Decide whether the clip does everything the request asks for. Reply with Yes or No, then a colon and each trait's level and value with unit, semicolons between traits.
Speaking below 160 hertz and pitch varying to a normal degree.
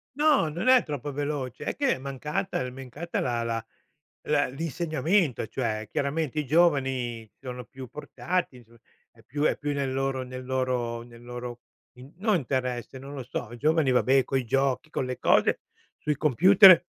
Yes: low, 135 Hz; average, 3.5 semitones